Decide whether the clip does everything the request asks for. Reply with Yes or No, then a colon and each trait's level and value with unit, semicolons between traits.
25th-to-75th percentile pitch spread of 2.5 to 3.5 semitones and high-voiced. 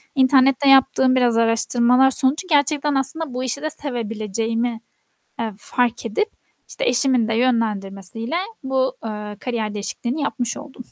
Yes: average, 3.0 semitones; very high, 250 Hz